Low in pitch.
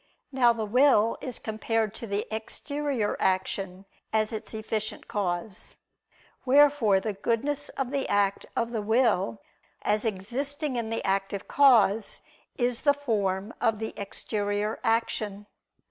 No: high, 220 Hz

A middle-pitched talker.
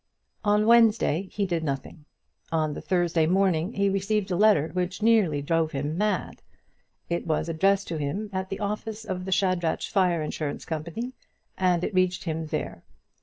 Yes: medium, 180 Hz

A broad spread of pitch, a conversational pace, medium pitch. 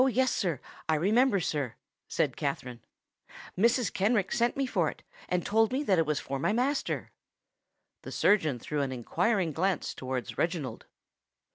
Yes: wide, 8.4 semitones; average, 150 wpm; medium, 180 Hz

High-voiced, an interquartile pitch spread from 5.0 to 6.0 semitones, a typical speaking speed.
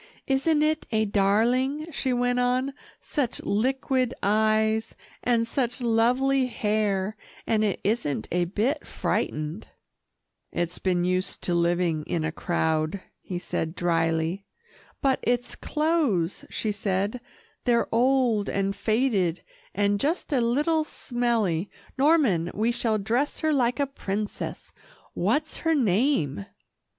No: high, 220 Hz; wide, 5.6 semitones; slow, 125 wpm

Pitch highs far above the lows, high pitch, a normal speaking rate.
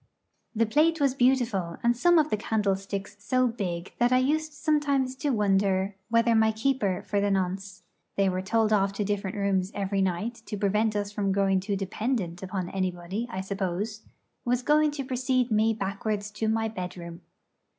No: average, 3.9 semitones; high, 210 Hz; average, 175 wpm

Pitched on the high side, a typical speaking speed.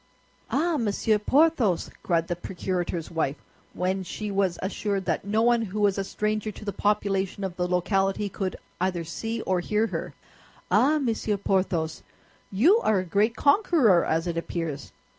Yes: high, 195 Hz; average, 160 wpm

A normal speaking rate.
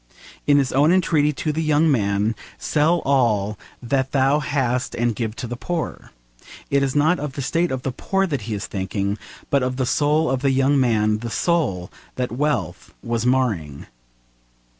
Yes: average, 180 wpm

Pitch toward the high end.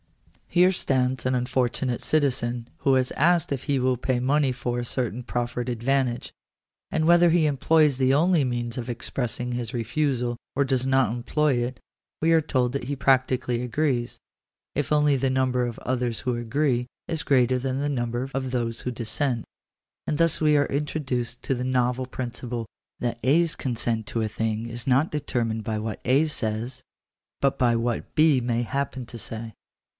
No: low, 125 Hz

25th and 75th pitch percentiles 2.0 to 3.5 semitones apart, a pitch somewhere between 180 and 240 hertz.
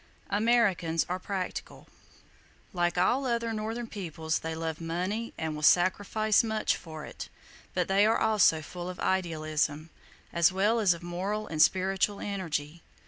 No: average, 4.4 semitones; medium, 185 Hz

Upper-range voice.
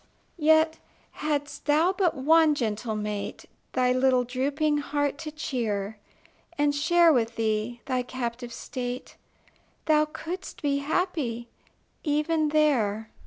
Yes: very high, 280 Hz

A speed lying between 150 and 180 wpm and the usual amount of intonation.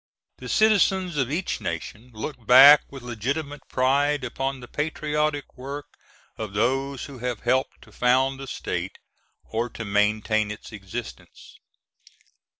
No: slow, 135 wpm; average, 4.0 semitones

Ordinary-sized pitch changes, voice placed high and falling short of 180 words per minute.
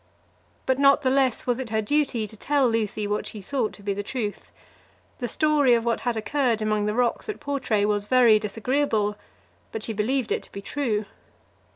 No: average, 3.9 semitones; high, 230 Hz; average, 200 wpm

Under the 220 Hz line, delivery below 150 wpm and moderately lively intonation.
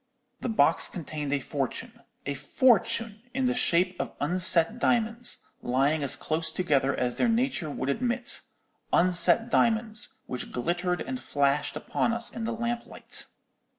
No: medium, 185 Hz; slow, 135 wpm; wide, 8.4 semitones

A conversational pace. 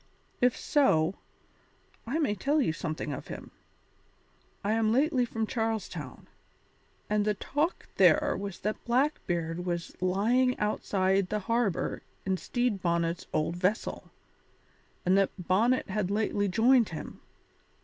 No: slow, 130 wpm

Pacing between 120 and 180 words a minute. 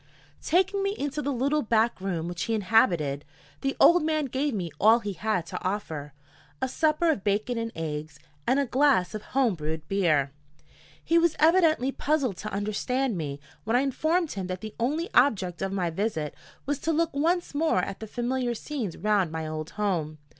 No: average, 190 wpm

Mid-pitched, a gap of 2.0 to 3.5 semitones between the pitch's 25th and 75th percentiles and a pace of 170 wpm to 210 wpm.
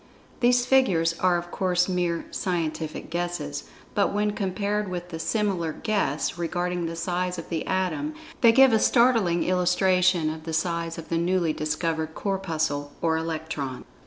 No: medium, 175 Hz; average, 2.8 semitones; average, 155 wpm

